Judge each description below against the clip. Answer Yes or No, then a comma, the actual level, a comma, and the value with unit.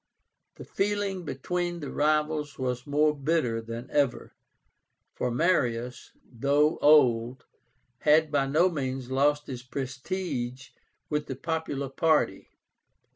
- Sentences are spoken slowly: Yes, slow, 115 wpm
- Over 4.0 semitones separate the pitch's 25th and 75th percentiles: No, average, 3.6 semitones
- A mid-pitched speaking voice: Yes, medium, 145 Hz